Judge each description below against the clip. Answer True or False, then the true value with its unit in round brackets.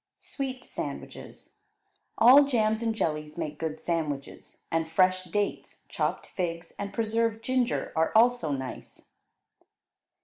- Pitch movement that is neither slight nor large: False (6.1 semitones)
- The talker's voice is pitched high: True (200 Hz)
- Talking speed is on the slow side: True (115 wpm)